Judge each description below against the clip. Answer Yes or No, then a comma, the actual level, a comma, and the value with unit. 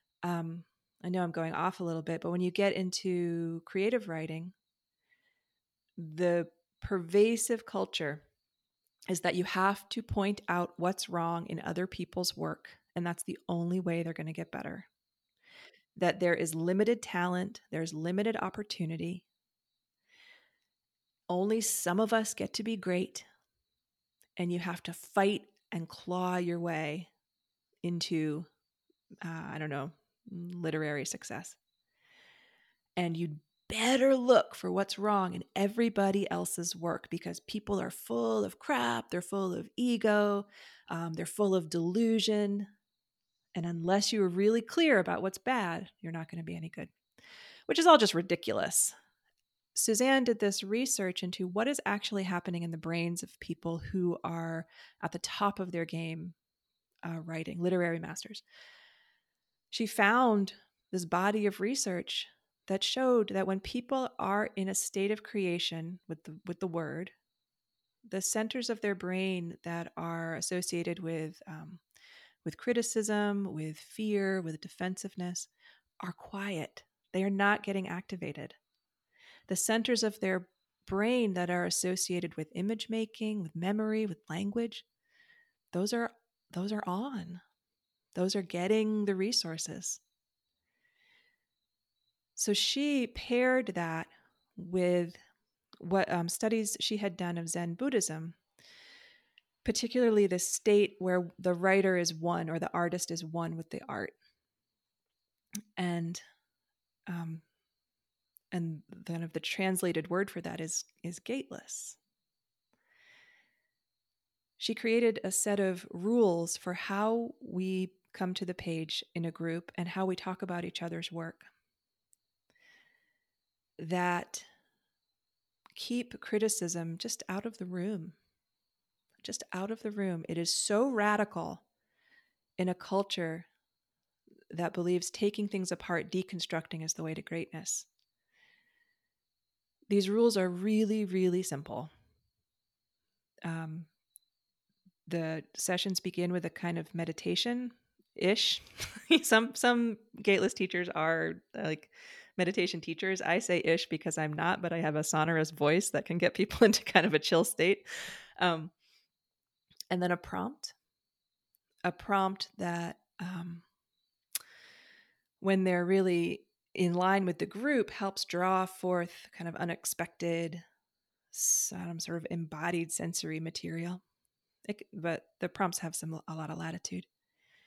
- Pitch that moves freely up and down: No, average, 4.0 semitones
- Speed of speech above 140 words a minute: No, slow, 135 wpm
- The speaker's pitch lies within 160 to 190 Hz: Yes, medium, 185 Hz